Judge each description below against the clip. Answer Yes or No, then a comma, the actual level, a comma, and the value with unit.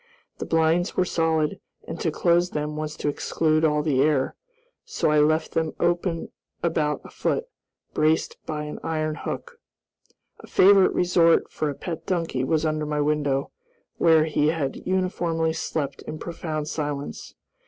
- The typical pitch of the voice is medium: Yes, medium, 155 Hz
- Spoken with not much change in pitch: Yes, narrow, 1.8 semitones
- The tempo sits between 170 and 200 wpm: No, average, 155 wpm